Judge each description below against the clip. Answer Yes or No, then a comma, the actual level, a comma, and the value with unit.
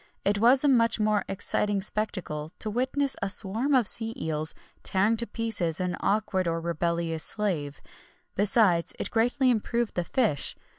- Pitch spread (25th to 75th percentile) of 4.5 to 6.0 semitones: Yes, average, 5.1 semitones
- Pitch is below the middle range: No, high, 205 Hz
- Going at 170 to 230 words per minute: No, average, 155 wpm